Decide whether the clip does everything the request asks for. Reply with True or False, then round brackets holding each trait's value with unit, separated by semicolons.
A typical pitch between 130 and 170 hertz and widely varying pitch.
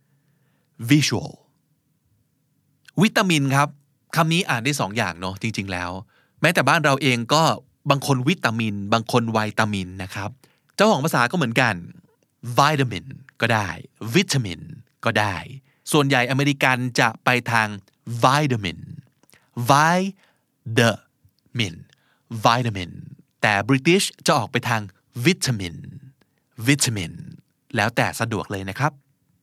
False (135 Hz; 4.3 semitones)